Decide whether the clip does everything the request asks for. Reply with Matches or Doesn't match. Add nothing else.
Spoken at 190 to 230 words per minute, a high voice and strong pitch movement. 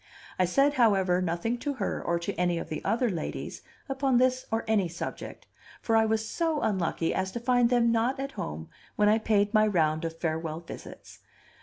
Matches